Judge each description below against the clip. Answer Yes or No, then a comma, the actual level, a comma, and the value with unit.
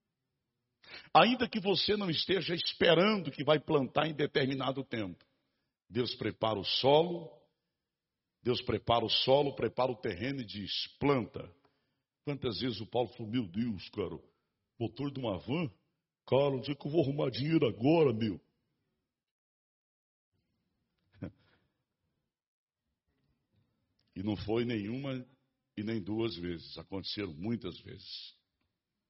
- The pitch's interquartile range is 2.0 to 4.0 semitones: No, average, 4.7 semitones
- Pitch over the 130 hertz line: No, low, 125 Hz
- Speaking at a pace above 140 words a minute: No, slow, 120 wpm